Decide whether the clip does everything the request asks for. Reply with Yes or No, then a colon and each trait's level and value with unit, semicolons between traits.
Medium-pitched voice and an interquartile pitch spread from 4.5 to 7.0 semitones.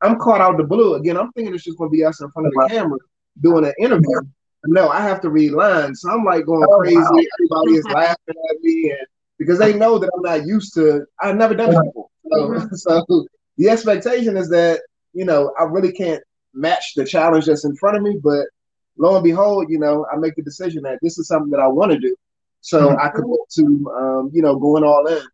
Yes: medium, 165 Hz; wide, 5.5 semitones